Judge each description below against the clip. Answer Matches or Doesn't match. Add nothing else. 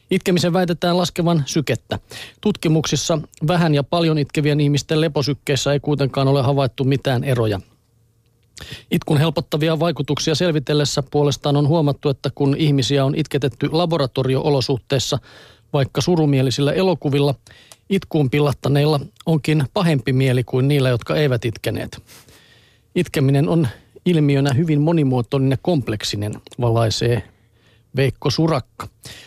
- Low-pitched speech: Doesn't match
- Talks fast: Doesn't match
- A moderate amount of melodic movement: Matches